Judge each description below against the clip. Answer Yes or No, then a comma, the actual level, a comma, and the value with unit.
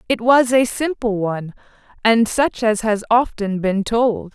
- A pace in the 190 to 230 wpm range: No, average, 165 wpm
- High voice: Yes, high, 225 Hz